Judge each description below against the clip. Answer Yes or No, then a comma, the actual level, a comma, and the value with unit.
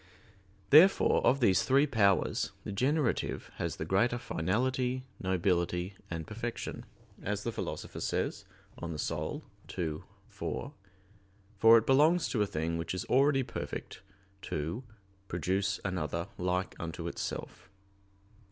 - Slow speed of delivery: Yes, slow, 125 wpm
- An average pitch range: No, wide, 6.4 semitones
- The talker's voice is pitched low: Yes, low, 100 Hz